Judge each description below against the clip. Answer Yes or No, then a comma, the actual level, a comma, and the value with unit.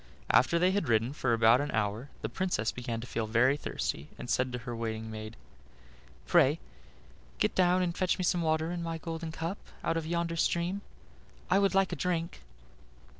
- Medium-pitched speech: Yes, medium, 160 Hz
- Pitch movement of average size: No, wide, 6.9 semitones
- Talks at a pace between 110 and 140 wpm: No, average, 190 wpm